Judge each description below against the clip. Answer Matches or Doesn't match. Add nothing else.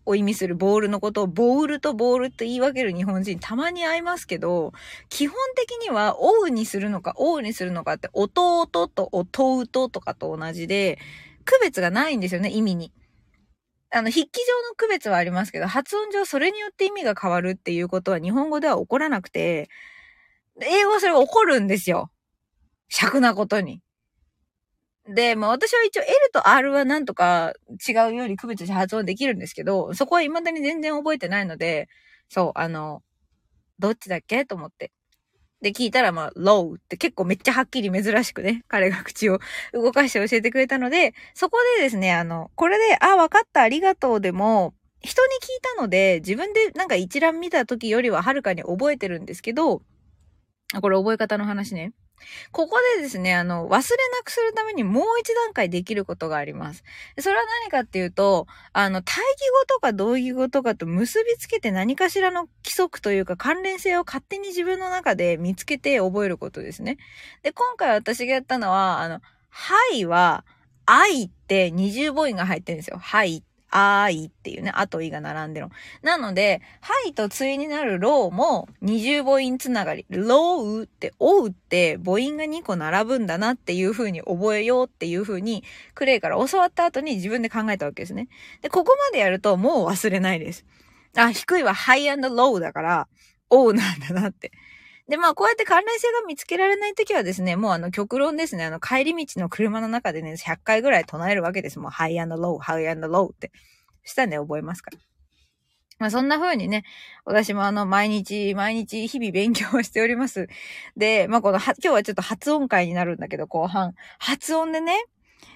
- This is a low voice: Doesn't match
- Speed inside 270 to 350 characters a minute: Doesn't match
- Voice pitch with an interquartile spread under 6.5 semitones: Doesn't match